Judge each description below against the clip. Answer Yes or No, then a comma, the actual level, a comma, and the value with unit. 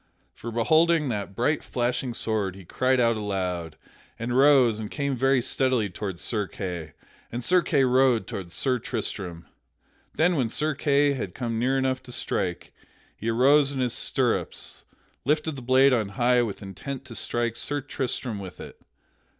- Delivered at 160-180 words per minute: Yes, average, 170 wpm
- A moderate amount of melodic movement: Yes, average, 4.2 semitones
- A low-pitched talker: Yes, low, 125 Hz